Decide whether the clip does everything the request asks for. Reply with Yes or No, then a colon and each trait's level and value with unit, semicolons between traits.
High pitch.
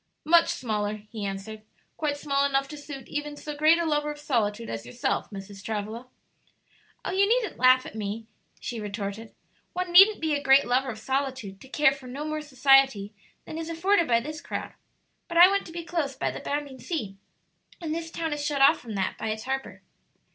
Yes: very high, 275 Hz